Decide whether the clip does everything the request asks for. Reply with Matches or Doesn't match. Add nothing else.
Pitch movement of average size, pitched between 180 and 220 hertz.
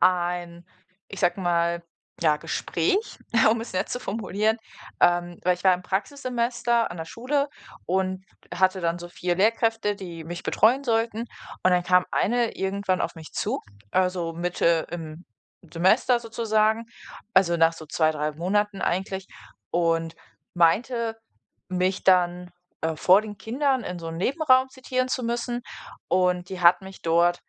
Matches